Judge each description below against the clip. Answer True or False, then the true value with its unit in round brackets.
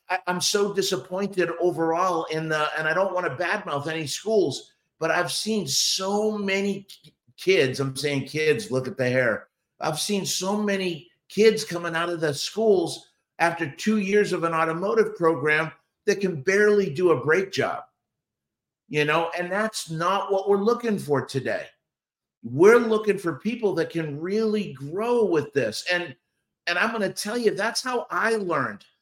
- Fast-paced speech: False (170 wpm)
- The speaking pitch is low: False (180 Hz)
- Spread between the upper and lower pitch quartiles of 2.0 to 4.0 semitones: False (4.5 semitones)